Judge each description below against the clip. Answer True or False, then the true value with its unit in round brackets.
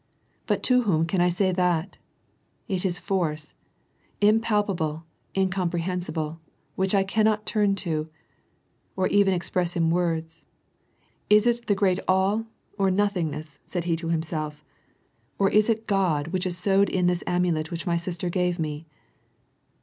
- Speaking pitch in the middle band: True (180 Hz)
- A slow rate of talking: False (155 wpm)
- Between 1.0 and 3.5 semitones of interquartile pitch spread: True (3.1 semitones)